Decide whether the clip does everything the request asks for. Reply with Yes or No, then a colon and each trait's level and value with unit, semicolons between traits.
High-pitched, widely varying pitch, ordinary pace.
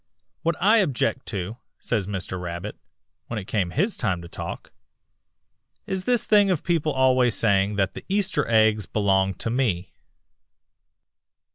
No: low, 115 Hz; wide, 8.9 semitones; average, 145 wpm